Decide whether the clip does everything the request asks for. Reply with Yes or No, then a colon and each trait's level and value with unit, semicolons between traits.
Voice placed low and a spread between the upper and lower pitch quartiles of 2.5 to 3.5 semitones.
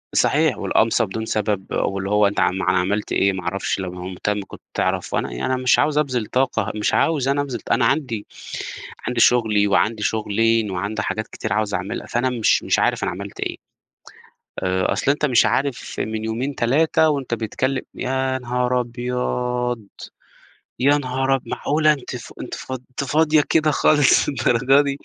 No: low, 120 Hz; average, 4.2 semitones